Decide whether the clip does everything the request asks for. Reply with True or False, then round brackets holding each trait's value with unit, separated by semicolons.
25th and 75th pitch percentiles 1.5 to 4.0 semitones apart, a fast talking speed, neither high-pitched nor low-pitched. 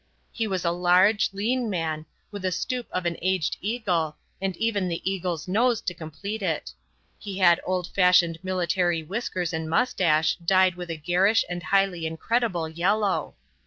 False (2.9 semitones; 160 wpm; 180 Hz)